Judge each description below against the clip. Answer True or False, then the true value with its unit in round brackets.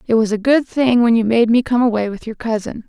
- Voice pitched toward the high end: True (230 Hz)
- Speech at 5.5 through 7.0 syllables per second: True (5.9 syllables/s)